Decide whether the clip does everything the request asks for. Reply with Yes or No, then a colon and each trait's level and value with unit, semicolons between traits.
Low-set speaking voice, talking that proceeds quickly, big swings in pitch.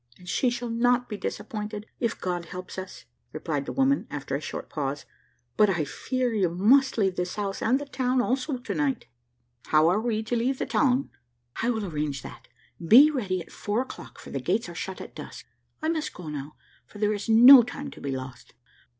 No: high, 215 Hz; fast, 210 wpm; wide, 6.1 semitones